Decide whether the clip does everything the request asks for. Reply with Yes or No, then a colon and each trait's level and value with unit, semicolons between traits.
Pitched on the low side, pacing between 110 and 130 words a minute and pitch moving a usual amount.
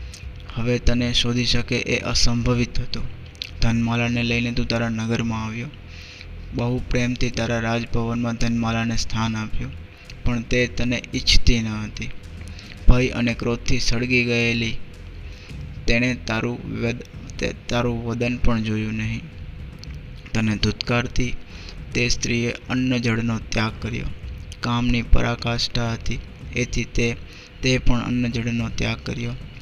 Yes: low, 115 Hz; average, 115 wpm; average, 3.1 semitones